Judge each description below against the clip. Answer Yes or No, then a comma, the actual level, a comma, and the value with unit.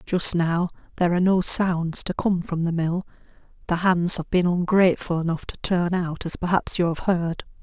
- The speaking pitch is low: No, medium, 175 Hz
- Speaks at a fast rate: No, average, 195 wpm